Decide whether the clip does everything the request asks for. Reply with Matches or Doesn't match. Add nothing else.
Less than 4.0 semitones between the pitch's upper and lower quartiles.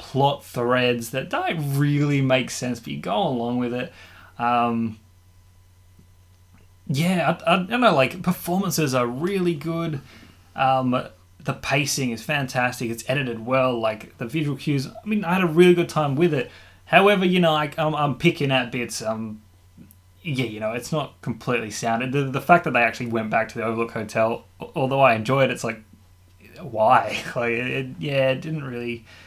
Doesn't match